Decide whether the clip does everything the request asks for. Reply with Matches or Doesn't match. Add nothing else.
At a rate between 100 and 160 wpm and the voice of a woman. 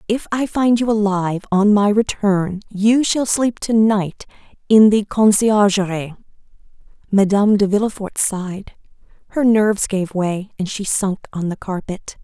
Matches